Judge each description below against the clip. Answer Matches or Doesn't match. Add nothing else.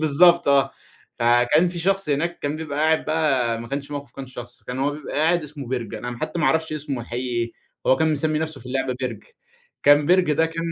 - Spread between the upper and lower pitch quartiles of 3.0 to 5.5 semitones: Matches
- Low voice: Doesn't match